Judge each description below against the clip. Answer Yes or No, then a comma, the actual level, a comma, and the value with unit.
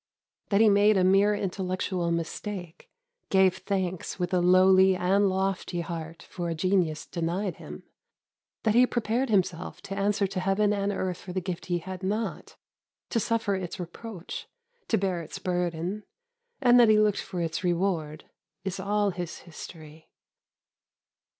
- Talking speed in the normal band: Yes, average, 155 wpm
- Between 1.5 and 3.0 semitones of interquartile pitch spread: Yes, narrow, 2.6 semitones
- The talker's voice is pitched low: No, medium, 185 Hz